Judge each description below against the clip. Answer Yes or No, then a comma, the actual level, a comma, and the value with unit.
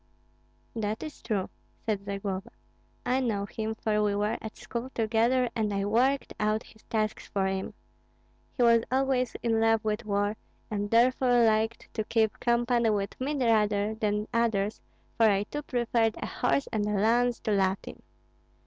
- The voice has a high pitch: Yes, high, 220 Hz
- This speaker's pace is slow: No, average, 165 wpm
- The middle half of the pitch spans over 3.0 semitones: No, narrow, 2.4 semitones